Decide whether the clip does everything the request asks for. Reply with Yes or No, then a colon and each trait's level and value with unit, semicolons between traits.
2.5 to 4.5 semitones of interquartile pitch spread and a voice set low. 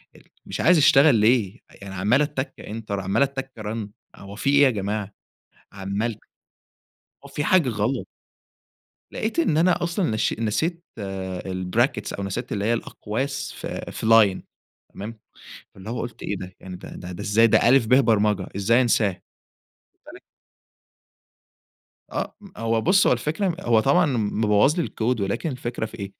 No: average, 5.0 semitones; low, 115 Hz